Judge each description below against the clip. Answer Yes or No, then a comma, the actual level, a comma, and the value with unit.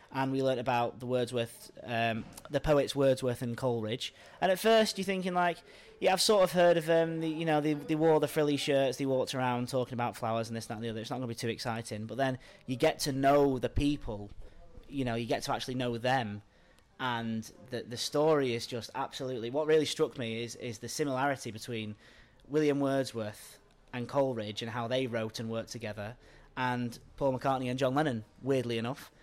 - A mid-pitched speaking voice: No, low, 125 Hz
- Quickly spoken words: Yes, fast, 215 wpm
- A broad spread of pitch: No, average, 3.5 semitones